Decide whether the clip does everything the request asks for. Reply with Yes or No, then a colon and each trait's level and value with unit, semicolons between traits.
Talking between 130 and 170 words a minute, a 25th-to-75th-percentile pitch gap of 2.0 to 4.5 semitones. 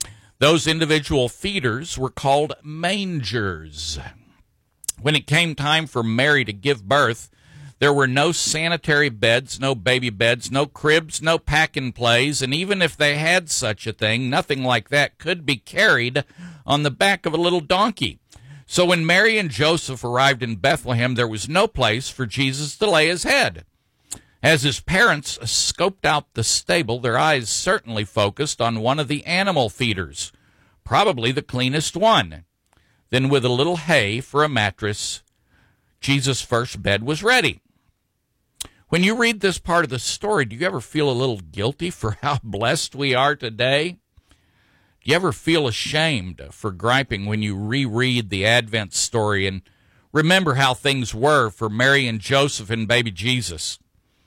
No: average, 165 wpm; average, 5.1 semitones